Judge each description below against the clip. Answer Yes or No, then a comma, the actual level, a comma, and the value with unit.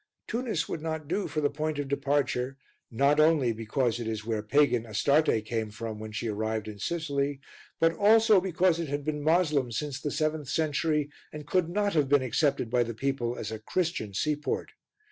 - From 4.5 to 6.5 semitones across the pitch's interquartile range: Yes, average, 5.2 semitones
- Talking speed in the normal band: Yes, average, 190 wpm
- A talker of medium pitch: Yes, medium, 145 Hz